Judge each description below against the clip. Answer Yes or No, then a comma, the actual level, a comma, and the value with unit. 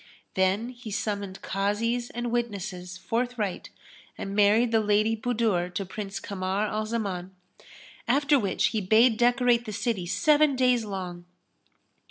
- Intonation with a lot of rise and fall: No, average, 3.4 semitones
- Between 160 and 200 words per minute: No, slow, 135 wpm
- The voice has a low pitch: No, high, 215 Hz